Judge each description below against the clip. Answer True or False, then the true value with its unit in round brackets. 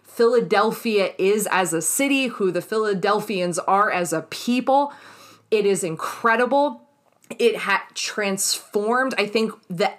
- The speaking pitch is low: False (210 Hz)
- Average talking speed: False (125 wpm)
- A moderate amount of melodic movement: True (4.1 semitones)